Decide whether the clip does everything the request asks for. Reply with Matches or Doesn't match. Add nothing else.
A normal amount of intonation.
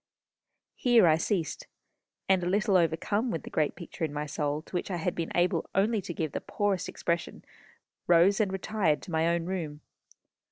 Matches